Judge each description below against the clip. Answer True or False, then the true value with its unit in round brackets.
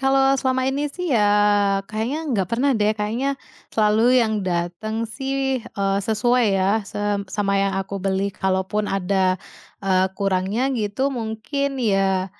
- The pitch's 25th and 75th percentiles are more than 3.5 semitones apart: True (4.3 semitones)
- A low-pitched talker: False (210 Hz)